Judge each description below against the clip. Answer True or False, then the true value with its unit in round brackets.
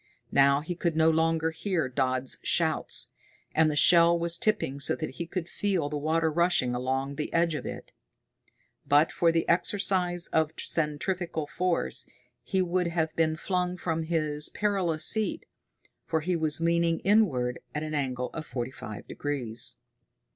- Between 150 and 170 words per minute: True (160 wpm)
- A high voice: False (160 Hz)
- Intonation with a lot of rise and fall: False (2.9 semitones)